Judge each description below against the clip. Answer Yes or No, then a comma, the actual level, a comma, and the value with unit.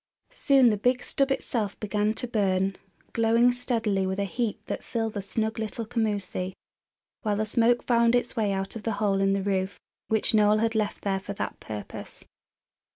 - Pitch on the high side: Yes, high, 215 Hz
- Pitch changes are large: No, average, 2.7 semitones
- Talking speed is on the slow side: No, average, 180 wpm